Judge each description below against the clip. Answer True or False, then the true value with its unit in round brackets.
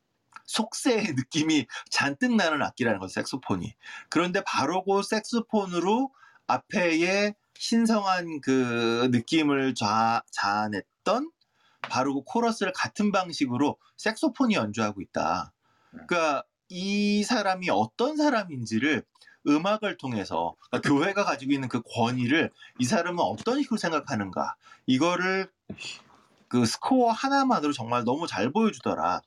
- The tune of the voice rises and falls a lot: True (9.0 semitones)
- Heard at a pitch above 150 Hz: True (190 Hz)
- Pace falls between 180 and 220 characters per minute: False (295 characters per minute)